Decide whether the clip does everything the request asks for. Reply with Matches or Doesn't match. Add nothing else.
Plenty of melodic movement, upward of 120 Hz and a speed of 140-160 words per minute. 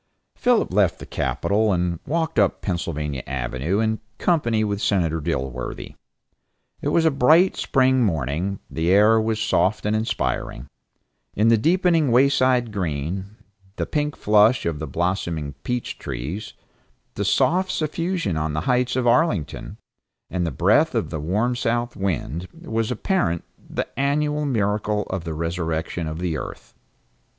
Doesn't match